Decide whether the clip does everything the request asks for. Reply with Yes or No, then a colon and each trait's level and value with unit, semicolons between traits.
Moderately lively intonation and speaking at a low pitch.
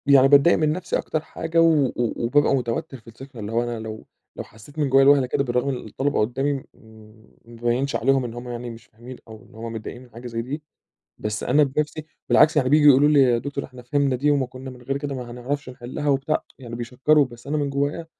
Yes: average, 3.0 semitones; low, 130 Hz